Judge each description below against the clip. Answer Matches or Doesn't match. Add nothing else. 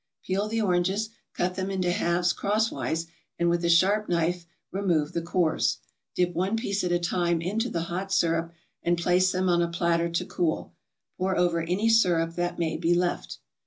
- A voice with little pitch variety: Matches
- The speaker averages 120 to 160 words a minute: Doesn't match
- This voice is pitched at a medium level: Matches